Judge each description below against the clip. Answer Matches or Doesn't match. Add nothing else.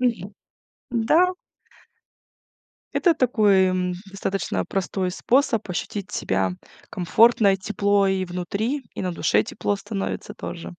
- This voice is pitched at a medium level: Doesn't match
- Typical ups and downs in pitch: Matches